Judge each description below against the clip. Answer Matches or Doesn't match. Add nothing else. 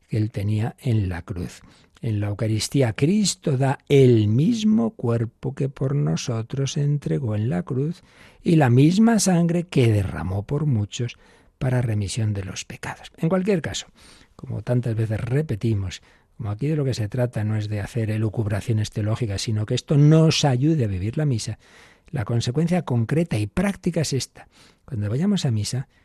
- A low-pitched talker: Matches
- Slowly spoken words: Doesn't match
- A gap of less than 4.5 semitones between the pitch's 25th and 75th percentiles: Doesn't match